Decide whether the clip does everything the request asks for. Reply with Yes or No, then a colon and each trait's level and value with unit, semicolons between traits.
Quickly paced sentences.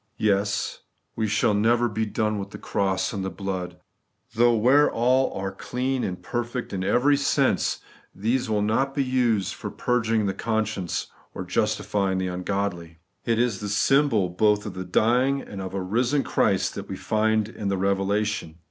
No: average, 175 wpm